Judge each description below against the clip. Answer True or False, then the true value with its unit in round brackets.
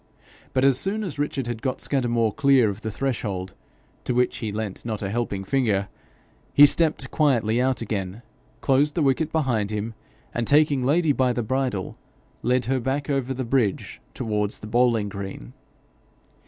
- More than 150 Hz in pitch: False (125 Hz)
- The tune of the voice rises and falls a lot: False (4.1 semitones)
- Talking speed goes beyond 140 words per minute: True (170 wpm)